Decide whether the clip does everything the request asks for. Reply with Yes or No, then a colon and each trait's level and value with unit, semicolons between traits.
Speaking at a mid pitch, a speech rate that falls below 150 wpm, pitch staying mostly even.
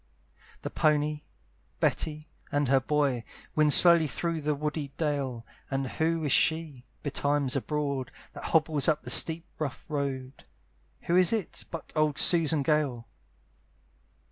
Yes: medium, 150 Hz; average, 140 wpm; narrow, 2.3 semitones